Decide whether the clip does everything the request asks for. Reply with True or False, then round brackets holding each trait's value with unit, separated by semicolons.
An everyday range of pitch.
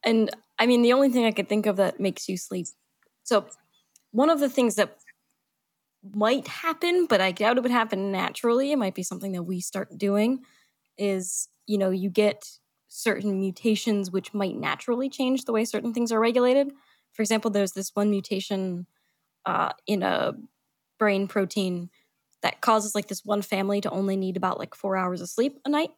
True (3.5 semitones)